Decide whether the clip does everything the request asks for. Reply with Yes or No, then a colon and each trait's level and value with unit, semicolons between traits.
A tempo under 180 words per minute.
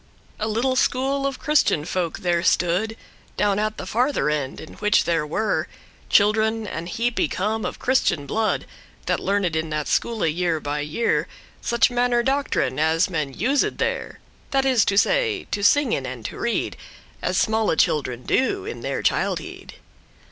Yes: average, 165 wpm